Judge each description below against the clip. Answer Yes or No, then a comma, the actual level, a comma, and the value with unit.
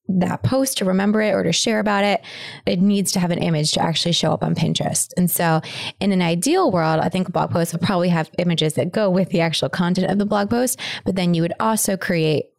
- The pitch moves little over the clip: No, average, 3.3 semitones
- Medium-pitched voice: Yes, medium, 180 Hz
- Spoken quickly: Yes, fast, 250 wpm